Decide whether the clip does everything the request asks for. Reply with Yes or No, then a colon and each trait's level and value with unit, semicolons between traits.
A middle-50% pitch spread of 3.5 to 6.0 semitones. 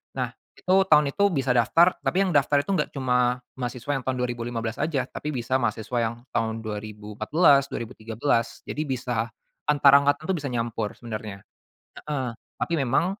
Yes: average, 4.1 semitones